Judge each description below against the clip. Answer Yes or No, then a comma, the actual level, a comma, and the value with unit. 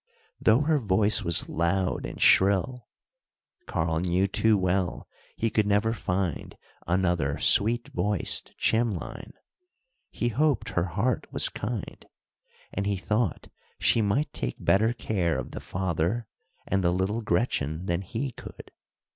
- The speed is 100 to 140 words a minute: Yes, slow, 135 wpm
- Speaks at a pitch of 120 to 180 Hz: No, low, 100 Hz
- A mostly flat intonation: No, average, 4.1 semitones